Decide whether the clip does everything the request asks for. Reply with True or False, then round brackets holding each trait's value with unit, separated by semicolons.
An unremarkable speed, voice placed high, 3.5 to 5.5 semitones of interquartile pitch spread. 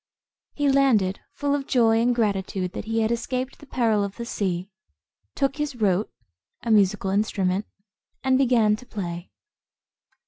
True (150 wpm; 225 Hz; 4.5 semitones)